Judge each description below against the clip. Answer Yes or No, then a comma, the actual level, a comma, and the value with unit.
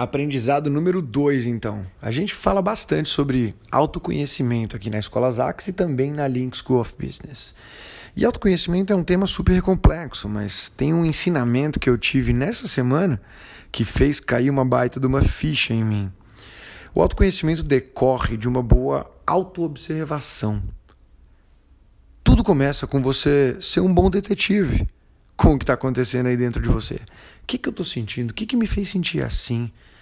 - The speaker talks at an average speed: Yes, average, 170 wpm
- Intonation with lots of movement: Yes, wide, 5.8 semitones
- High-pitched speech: No, low, 135 Hz